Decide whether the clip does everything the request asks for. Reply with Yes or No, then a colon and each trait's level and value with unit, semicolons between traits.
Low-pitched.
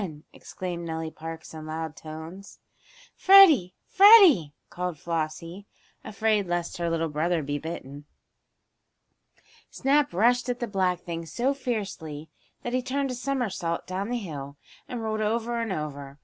No: medium, 180 Hz